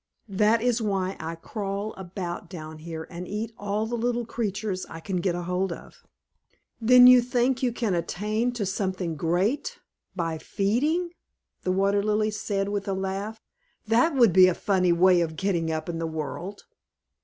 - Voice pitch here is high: Yes, high, 195 Hz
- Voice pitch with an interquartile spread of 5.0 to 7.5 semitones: No, average, 3.9 semitones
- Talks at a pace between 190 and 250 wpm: No, average, 175 wpm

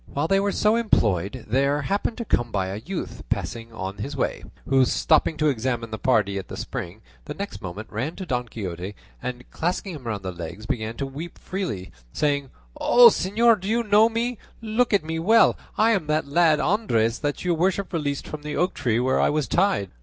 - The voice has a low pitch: No, medium, 145 Hz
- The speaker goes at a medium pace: No, fast, 215 wpm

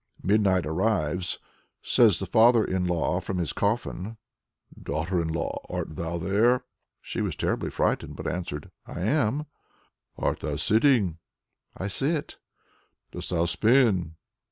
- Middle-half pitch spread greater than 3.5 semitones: Yes, average, 4.8 semitones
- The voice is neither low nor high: No, very low, 95 Hz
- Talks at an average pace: No, slow, 130 wpm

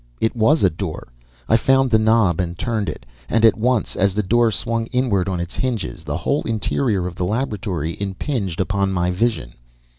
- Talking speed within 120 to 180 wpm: No, average, 190 wpm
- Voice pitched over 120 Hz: No, low, 105 Hz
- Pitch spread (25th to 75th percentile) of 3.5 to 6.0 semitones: Yes, average, 4.3 semitones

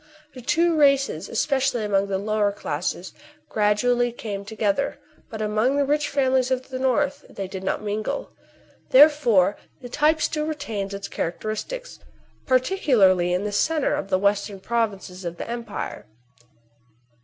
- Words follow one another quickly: No, average, 145 wpm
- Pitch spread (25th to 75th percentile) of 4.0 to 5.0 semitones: No, wide, 5.6 semitones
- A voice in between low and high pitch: No, high, 225 Hz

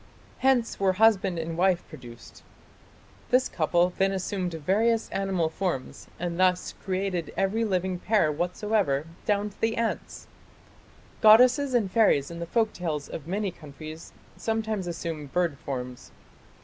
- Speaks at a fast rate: No, slow, 135 wpm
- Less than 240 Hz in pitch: Yes, medium, 185 Hz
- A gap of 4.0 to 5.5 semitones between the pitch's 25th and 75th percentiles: Yes, average, 4.4 semitones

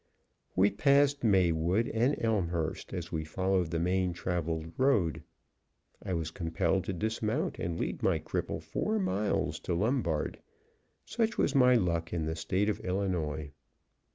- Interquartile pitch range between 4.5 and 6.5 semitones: Yes, average, 4.8 semitones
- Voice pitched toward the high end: No, very low, 95 Hz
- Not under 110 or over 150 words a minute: Yes, average, 145 wpm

